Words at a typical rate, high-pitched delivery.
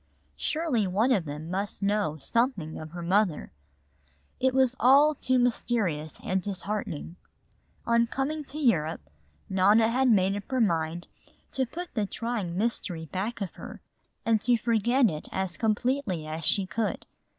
Yes: average, 150 wpm; high, 210 Hz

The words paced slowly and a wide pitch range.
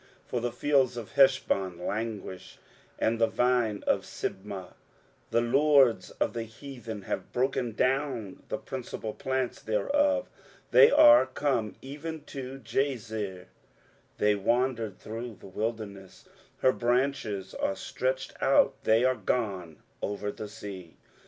No: slow, 130 wpm; average, 4.2 semitones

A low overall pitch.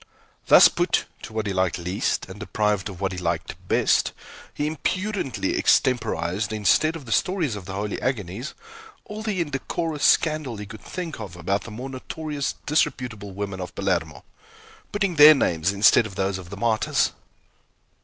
Yes: low, 110 Hz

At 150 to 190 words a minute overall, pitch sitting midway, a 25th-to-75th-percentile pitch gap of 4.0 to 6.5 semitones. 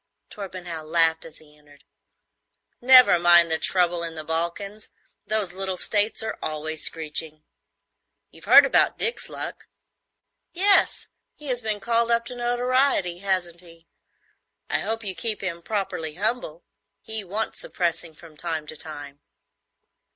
No: average, 140 wpm; medium, 175 Hz; average, 5.2 semitones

